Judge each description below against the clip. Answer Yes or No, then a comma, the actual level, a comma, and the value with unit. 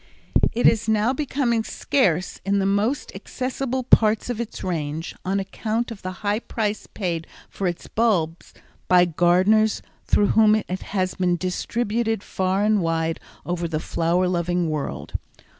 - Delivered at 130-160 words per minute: Yes, average, 150 wpm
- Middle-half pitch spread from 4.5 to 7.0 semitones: No, average, 4.0 semitones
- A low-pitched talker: No, high, 195 Hz